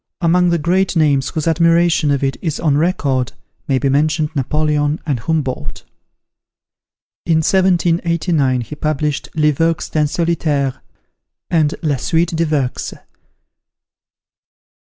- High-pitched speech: No, medium, 155 Hz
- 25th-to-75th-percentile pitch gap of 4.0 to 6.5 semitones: No, average, 2.8 semitones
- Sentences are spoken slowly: Yes, slow, 120 wpm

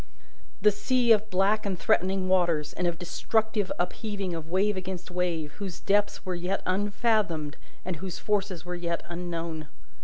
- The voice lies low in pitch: No, medium, 185 Hz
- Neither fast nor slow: Yes, average, 155 wpm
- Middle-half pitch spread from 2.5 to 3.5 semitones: Yes, average, 3.0 semitones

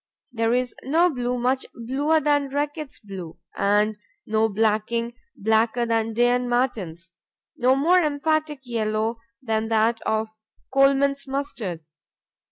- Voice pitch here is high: Yes, high, 240 Hz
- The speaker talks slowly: Yes, slow, 125 wpm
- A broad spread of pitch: No, average, 4.0 semitones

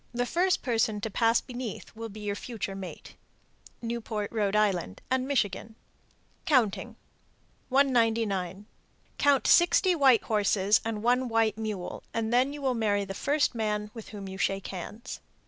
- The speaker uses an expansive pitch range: No, average, 3.4 semitones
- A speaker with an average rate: Yes, average, 145 wpm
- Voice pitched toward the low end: No, high, 225 Hz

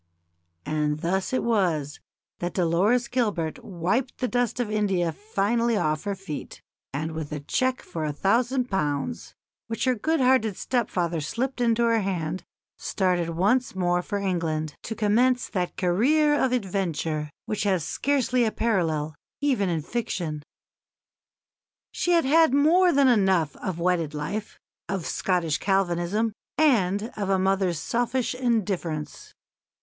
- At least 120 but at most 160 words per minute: Yes, average, 140 wpm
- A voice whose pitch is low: No, high, 195 Hz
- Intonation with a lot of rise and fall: Yes, wide, 6.1 semitones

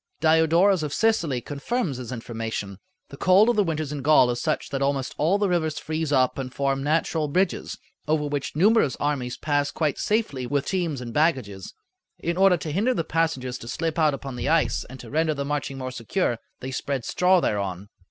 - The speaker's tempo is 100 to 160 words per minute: No, average, 200 wpm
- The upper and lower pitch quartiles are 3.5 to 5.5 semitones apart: Yes, average, 4.3 semitones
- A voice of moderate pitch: Yes, medium, 145 Hz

